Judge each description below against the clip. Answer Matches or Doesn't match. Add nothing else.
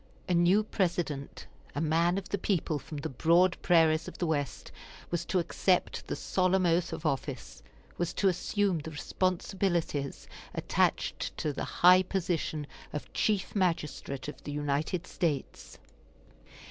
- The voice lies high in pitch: Doesn't match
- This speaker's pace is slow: Doesn't match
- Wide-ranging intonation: Doesn't match